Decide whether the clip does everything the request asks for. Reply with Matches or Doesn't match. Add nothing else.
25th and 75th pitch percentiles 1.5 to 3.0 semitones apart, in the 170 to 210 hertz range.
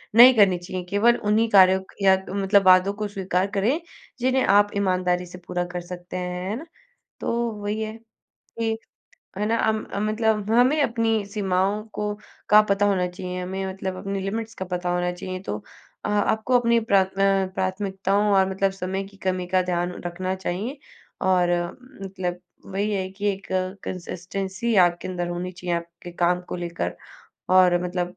Matches